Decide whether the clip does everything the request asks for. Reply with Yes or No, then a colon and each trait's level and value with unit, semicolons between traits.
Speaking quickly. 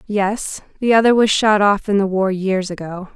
Yes: fast, 210 wpm